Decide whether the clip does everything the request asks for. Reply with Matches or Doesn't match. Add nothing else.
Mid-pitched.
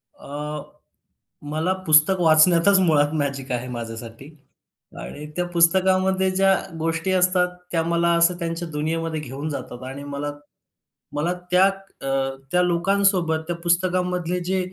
Matches